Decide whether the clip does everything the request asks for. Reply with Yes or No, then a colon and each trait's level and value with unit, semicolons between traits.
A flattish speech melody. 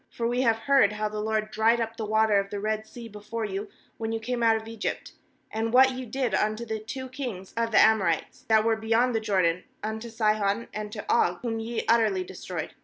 Yes: narrow, 1.6 semitones